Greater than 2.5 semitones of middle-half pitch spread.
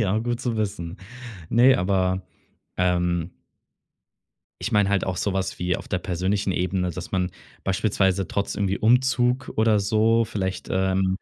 Yes: average, 2.9 semitones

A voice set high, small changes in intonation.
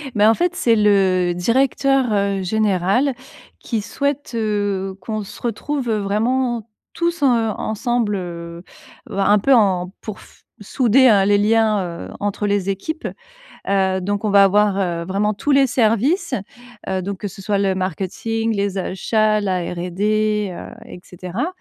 No: high, 205 Hz; average, 3.0 semitones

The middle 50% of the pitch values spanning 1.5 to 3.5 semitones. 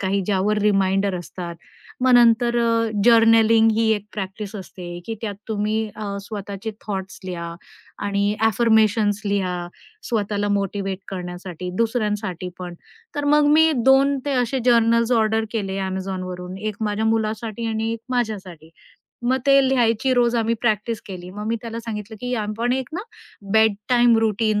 Yes: average, 2.9 semitones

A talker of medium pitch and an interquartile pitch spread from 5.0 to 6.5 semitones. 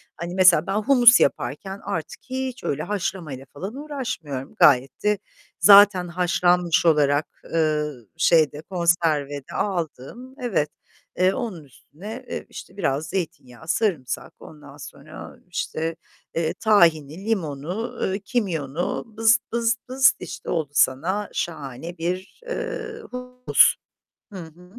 Yes: medium, 175 Hz; wide, 5.5 semitones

